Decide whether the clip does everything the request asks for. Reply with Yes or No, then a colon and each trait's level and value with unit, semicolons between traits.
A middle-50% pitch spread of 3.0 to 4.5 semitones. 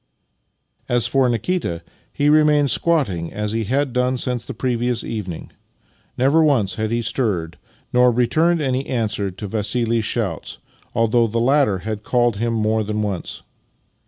Yes: average, 3.5 semitones